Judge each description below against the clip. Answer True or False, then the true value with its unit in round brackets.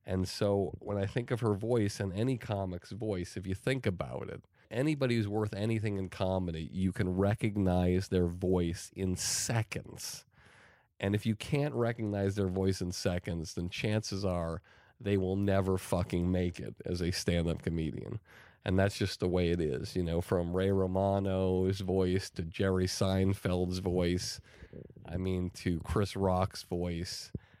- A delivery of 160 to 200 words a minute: True (165 wpm)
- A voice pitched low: True (95 Hz)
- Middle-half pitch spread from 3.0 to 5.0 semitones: False (2.4 semitones)